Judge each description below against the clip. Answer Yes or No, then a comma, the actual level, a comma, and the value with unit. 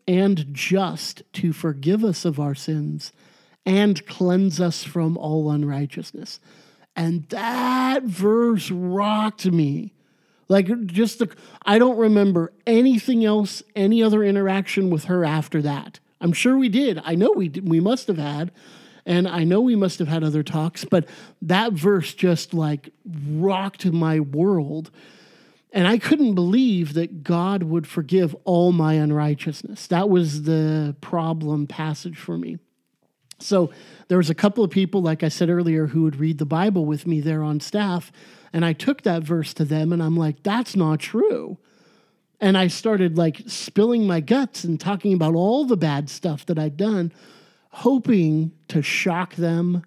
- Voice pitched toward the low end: No, medium, 175 Hz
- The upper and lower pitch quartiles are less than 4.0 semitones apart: No, average, 4.4 semitones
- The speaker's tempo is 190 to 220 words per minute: No, average, 165 wpm